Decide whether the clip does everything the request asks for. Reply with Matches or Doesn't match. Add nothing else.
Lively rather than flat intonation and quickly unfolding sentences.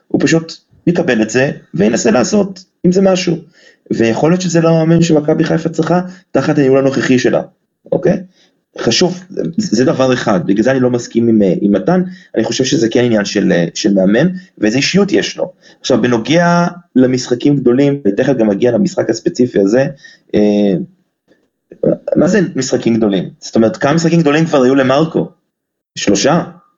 Matches